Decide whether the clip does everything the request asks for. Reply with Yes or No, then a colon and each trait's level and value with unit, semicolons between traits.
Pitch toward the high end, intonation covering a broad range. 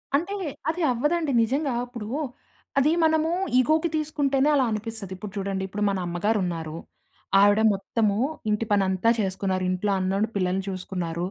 Yes: high, 210 Hz; wide, 6.5 semitones